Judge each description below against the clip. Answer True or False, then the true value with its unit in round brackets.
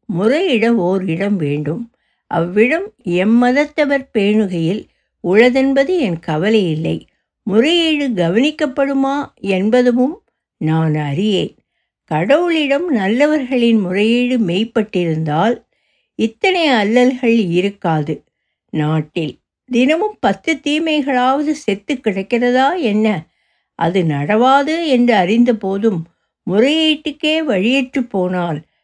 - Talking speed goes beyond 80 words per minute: False (75 wpm)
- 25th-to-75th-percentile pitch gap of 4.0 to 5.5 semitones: False (6.8 semitones)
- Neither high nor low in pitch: False (230 Hz)